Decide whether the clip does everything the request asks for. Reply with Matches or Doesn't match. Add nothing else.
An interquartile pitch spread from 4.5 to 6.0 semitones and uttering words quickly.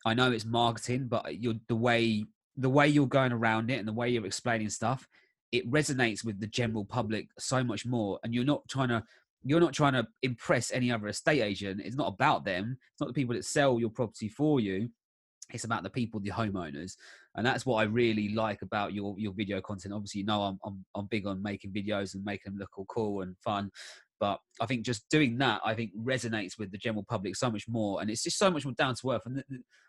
Doesn't match